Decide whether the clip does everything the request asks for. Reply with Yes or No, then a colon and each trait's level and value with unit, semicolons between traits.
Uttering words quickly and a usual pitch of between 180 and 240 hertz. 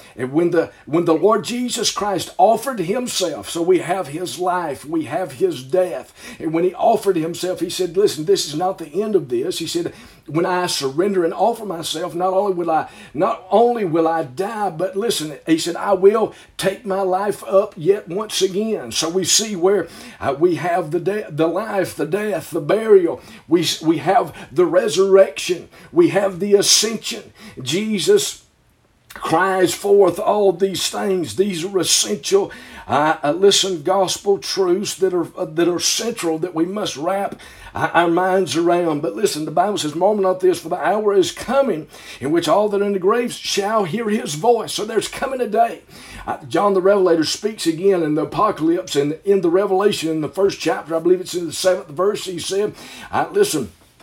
No: average, 190 wpm; high, 190 Hz